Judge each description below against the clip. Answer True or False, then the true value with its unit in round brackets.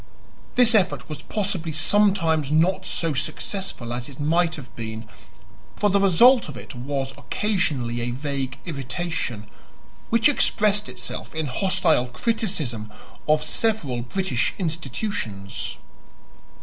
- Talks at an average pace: False (120 wpm)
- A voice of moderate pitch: True (155 Hz)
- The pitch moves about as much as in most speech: False (7.5 semitones)